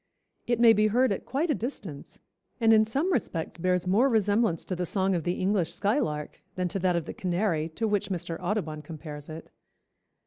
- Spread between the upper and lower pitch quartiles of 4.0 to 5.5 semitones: Yes, average, 4.7 semitones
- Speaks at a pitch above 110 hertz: Yes, high, 190 Hz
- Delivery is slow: No, average, 200 wpm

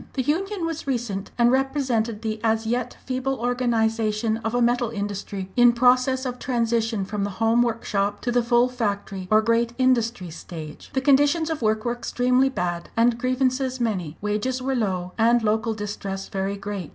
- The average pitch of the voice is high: Yes, high, 230 Hz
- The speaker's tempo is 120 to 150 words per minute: No, average, 175 wpm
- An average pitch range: Yes, average, 3.4 semitones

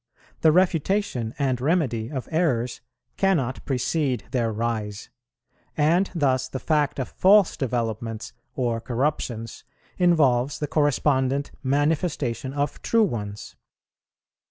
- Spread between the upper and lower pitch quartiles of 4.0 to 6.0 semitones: Yes, average, 4.6 semitones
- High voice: No, low, 135 Hz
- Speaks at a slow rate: Yes, slow, 110 wpm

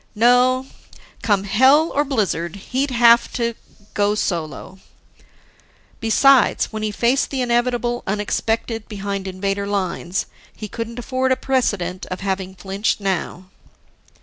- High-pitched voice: Yes, high, 215 Hz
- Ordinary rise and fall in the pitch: Yes, average, 4.2 semitones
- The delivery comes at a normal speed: No, slow, 120 wpm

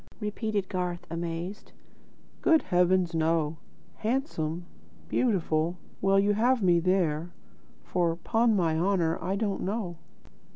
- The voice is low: No, medium, 180 Hz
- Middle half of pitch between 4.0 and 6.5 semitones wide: No, average, 3.6 semitones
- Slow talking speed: Yes, slow, 115 wpm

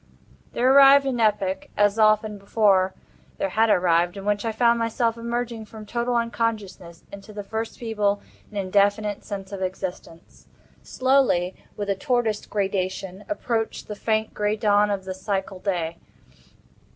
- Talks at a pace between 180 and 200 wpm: No, slow, 135 wpm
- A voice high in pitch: Yes, high, 210 Hz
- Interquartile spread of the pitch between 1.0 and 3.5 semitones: Yes, average, 2.9 semitones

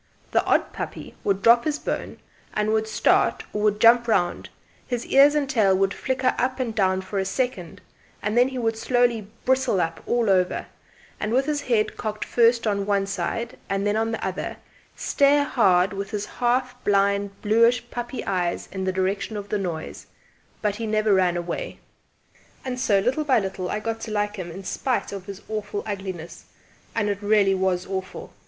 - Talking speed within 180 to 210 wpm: Yes, average, 190 wpm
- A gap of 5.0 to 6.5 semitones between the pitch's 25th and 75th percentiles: No, average, 3.6 semitones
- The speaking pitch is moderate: No, high, 210 Hz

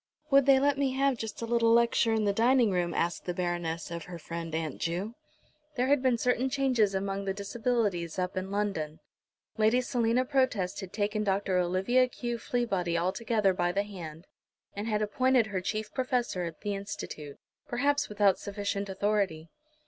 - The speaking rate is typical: Yes, average, 175 wpm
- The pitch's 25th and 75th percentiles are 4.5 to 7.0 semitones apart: Yes, average, 4.8 semitones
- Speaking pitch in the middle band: No, high, 205 Hz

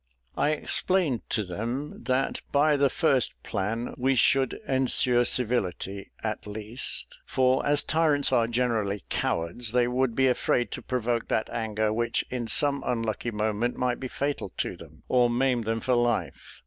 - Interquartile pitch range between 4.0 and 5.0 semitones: No, average, 2.9 semitones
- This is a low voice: Yes, low, 120 Hz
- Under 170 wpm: Yes, average, 160 wpm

